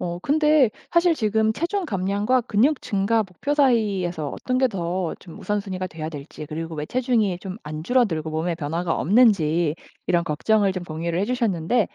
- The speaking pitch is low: No, high, 195 Hz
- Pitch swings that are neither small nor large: No, wide, 6.2 semitones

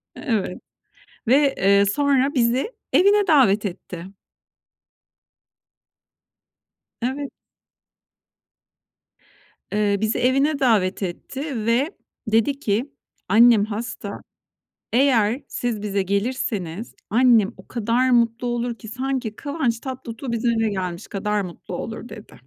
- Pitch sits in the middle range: No, high, 230 Hz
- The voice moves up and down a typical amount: Yes, average, 4.1 semitones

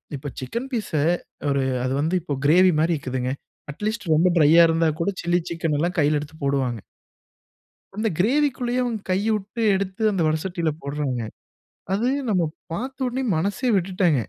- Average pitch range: No, wide, 6.1 semitones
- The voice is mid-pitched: Yes, medium, 175 Hz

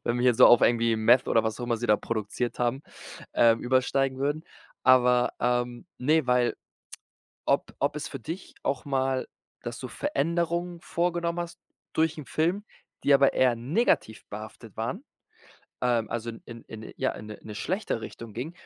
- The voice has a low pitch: Yes, low, 125 Hz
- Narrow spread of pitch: No, average, 4.7 semitones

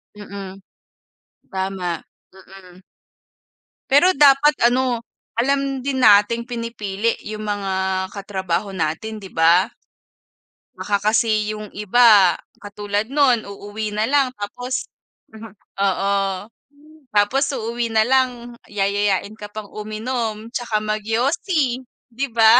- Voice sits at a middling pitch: No, high, 215 Hz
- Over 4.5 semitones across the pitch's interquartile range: No, average, 3.3 semitones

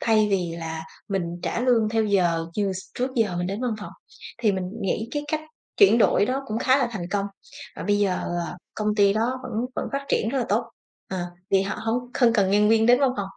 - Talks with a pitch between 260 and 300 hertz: No, high, 210 Hz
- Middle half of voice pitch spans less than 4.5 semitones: Yes, average, 3.9 semitones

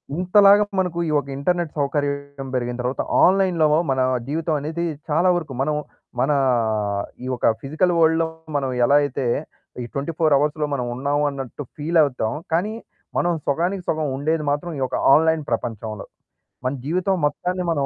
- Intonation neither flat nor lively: Yes, average, 3.6 semitones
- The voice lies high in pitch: No, medium, 150 Hz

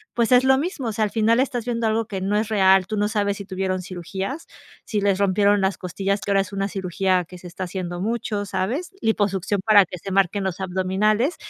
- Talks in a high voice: Yes, high, 200 Hz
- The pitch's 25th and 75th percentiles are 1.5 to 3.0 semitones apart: Yes, narrow, 2.6 semitones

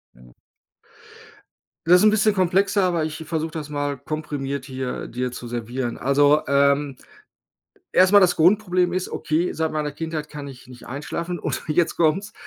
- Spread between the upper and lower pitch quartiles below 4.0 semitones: No, average, 4.3 semitones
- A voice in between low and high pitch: Yes, medium, 155 Hz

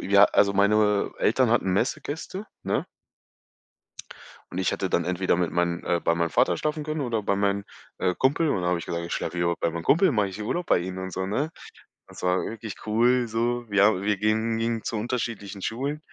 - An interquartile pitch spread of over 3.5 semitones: Yes, average, 4.3 semitones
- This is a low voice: Yes, low, 105 Hz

